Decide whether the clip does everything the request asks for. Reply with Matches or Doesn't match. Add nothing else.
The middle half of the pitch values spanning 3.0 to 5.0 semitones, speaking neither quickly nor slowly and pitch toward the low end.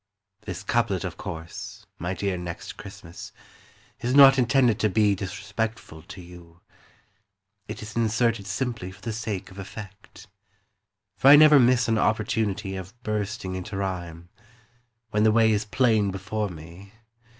Matches